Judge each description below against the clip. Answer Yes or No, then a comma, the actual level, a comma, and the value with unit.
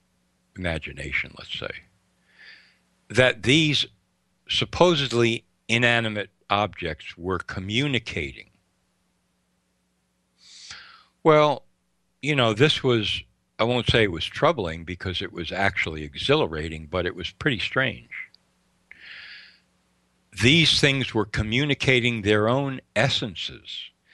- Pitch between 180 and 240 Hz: No, low, 105 Hz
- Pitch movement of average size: No, wide, 7.6 semitones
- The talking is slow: Yes, slow, 95 wpm